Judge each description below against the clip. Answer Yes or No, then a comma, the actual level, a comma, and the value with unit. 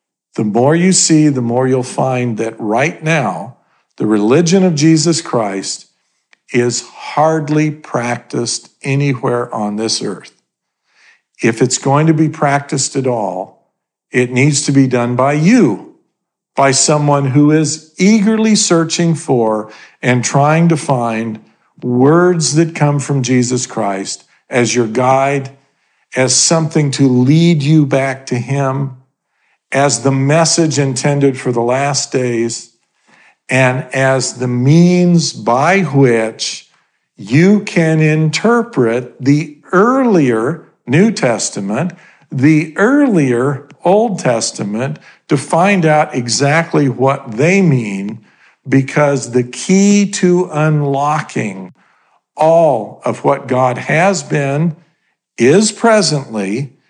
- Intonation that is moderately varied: Yes, average, 4.4 semitones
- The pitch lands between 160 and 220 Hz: No, medium, 140 Hz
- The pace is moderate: No, slow, 115 wpm